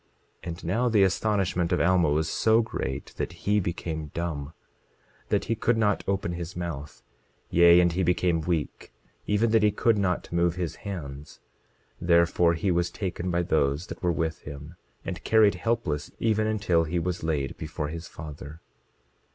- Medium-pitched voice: No, very low, 85 Hz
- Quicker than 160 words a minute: Yes, average, 170 wpm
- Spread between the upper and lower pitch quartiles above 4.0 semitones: No, average, 3.5 semitones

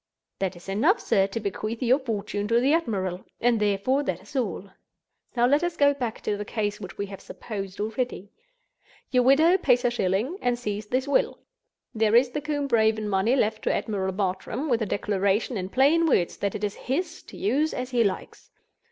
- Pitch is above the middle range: Yes, high, 225 Hz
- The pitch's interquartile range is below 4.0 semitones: No, average, 4.8 semitones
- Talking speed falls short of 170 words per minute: No, average, 200 wpm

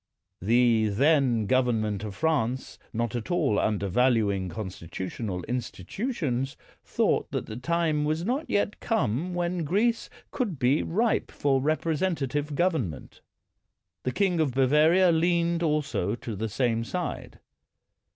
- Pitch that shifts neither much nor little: No, wide, 7.1 semitones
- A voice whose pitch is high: No, low, 135 Hz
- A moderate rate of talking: No, slow, 130 wpm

